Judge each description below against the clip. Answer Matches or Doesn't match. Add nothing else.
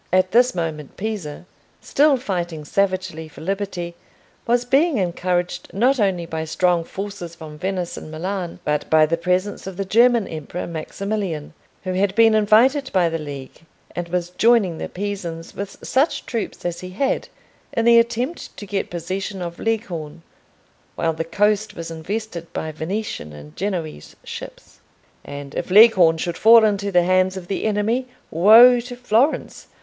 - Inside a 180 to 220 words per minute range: Doesn't match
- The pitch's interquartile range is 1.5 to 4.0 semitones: Doesn't match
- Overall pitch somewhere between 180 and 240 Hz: Matches